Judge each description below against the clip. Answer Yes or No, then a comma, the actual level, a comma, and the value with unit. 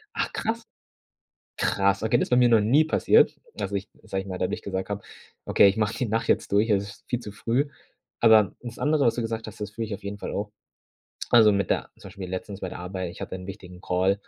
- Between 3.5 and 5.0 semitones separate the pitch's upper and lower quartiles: No, average, 2.9 semitones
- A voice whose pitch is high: No, low, 105 Hz